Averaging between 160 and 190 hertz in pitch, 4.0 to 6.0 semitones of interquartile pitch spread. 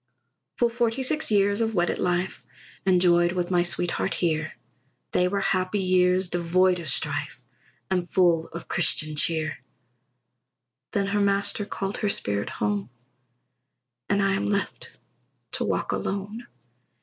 No: medium, 185 Hz; average, 2.7 semitones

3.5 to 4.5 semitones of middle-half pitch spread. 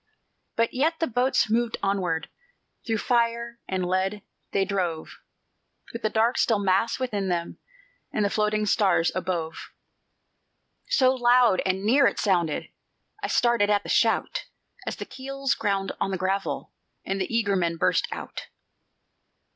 Yes: average, 3.9 semitones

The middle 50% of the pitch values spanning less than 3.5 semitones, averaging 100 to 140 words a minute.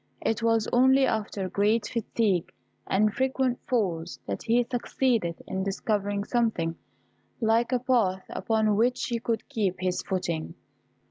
No: average, 4.1 semitones; slow, 135 wpm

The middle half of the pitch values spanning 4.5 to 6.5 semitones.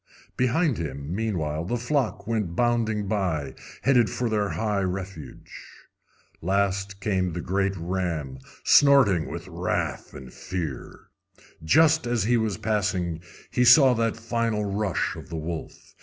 Yes: average, 5.0 semitones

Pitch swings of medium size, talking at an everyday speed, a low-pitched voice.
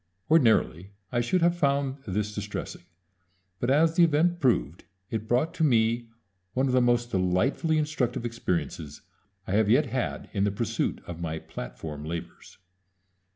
No: wide, 6.7 semitones; average, 155 wpm; low, 120 Hz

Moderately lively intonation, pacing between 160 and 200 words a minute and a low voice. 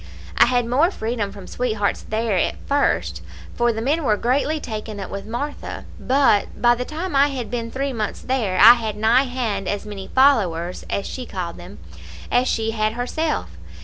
No: average, 3.8 semitones; average, 185 wpm; high, 235 Hz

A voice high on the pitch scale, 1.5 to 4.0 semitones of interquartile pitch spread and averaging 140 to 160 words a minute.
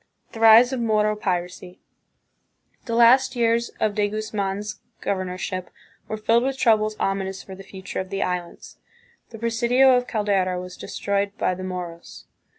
Yes: high, 210 Hz; average, 3.5 semitones; average, 155 wpm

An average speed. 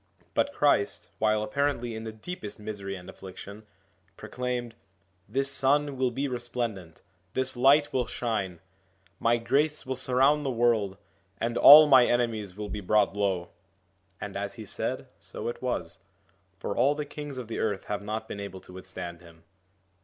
Yes: average, 170 wpm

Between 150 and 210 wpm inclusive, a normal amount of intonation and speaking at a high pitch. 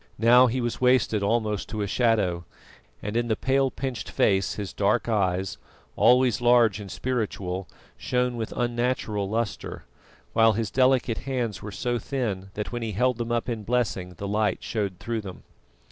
No: average, 170 wpm; average, 3.3 semitones; low, 115 Hz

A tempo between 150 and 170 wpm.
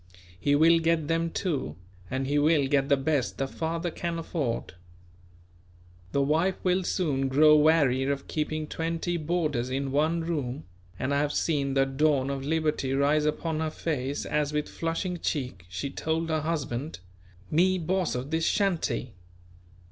Yes: average, 160 wpm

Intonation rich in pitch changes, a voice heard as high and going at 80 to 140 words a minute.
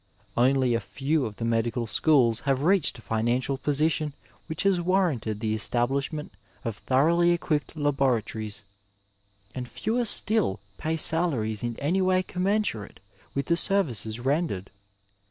No: wide, 6.5 semitones; low, 135 Hz; slow, 135 wpm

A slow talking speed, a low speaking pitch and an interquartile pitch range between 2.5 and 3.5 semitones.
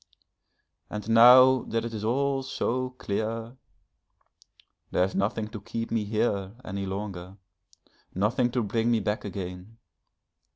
Yes: slow, 130 wpm; low, 110 Hz; average, 3.1 semitones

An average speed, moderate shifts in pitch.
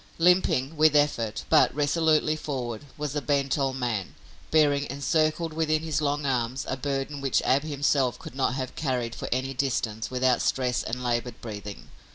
Yes: average, 170 wpm; average, 3.1 semitones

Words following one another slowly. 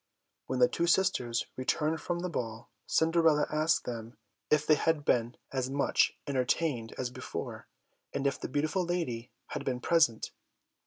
No: average, 155 wpm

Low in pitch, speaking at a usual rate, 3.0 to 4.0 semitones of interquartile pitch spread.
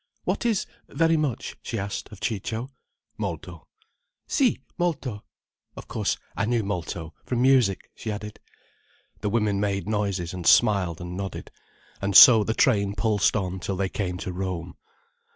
Yes: low, 100 Hz; average, 150 wpm; average, 3.5 semitones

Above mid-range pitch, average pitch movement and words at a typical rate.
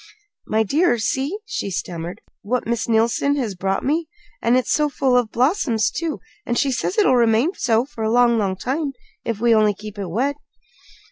Yes: high, 235 Hz; average, 4.3 semitones; average, 190 wpm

